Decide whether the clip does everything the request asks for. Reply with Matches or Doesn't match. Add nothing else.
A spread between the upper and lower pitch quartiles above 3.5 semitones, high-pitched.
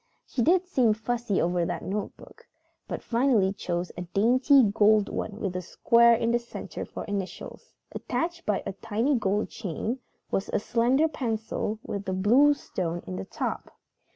Matches